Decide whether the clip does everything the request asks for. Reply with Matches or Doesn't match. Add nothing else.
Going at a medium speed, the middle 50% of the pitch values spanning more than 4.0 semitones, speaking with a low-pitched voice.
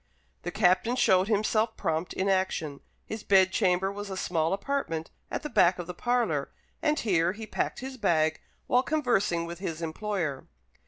Doesn't match